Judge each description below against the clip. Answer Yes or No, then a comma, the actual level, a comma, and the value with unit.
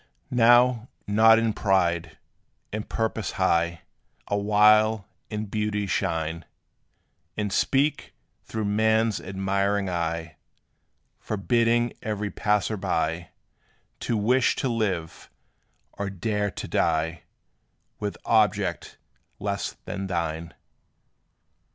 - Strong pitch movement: No, average, 3.4 semitones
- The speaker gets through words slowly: Yes, slow, 95 wpm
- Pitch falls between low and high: No, low, 105 Hz